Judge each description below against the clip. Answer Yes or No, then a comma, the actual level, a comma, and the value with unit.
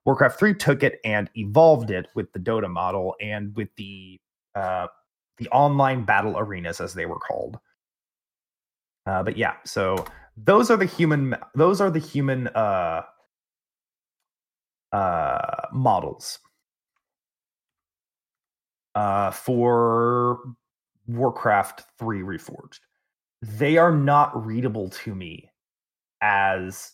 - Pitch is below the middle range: Yes, low, 120 Hz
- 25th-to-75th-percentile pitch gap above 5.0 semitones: Yes, wide, 5.5 semitones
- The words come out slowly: Yes, slow, 110 wpm